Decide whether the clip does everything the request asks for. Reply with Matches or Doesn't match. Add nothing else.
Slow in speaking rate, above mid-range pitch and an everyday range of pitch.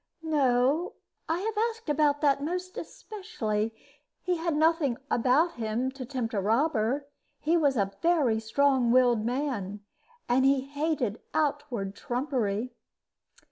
Matches